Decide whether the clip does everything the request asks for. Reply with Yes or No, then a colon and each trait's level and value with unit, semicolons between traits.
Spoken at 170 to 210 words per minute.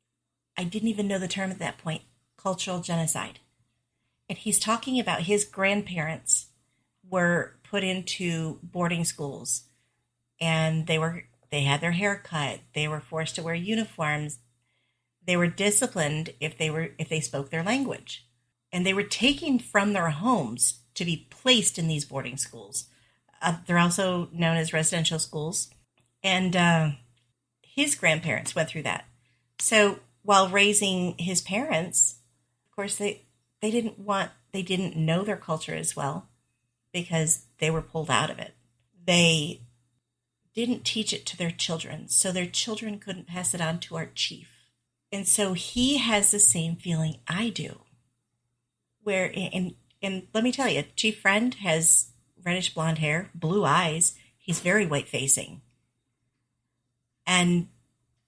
No: average, 150 wpm